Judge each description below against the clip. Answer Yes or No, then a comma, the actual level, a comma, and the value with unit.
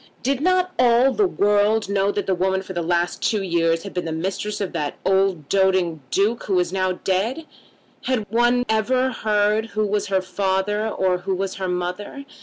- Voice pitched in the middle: No, high, 195 Hz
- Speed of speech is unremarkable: Yes, average, 195 wpm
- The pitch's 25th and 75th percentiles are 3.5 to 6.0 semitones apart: No, average, 3.1 semitones